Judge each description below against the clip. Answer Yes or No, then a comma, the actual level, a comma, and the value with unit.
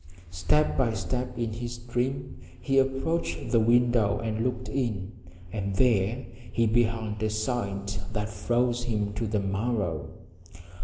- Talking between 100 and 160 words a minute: Yes, average, 140 wpm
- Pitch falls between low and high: No, low, 115 Hz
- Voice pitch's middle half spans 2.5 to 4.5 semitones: Yes, average, 2.9 semitones